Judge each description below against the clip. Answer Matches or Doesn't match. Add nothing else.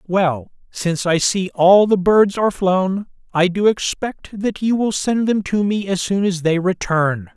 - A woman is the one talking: Doesn't match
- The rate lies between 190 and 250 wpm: Matches